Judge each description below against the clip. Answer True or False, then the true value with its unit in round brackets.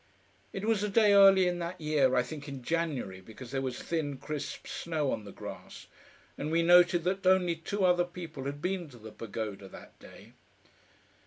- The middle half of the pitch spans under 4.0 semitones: False (5.3 semitones)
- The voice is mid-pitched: True (160 Hz)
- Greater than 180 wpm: True (190 wpm)